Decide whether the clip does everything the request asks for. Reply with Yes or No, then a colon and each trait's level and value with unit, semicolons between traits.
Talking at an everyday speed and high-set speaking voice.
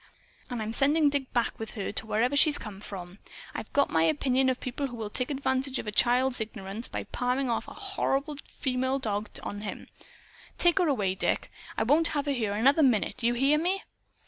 No: fast, 210 wpm; very high, 250 Hz